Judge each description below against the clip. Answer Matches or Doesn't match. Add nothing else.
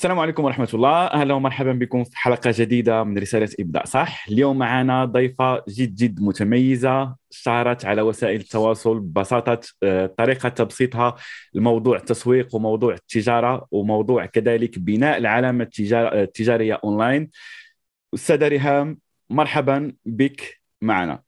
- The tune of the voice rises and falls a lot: Doesn't match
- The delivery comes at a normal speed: Matches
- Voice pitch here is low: Matches